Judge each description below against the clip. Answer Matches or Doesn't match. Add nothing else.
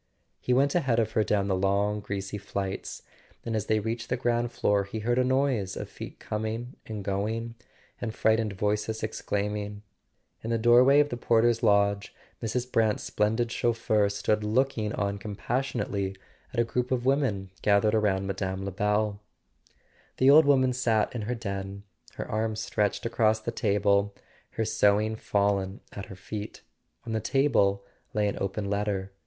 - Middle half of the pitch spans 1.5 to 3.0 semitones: Matches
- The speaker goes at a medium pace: Matches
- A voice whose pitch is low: Matches